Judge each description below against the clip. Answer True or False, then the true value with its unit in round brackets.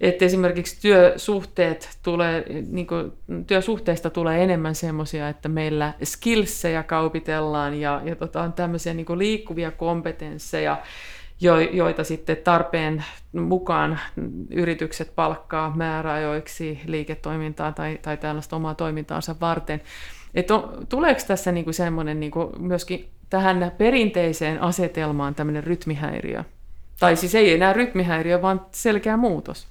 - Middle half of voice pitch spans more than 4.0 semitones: False (2.4 semitones)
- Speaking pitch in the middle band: True (165 Hz)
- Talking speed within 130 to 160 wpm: False (115 wpm)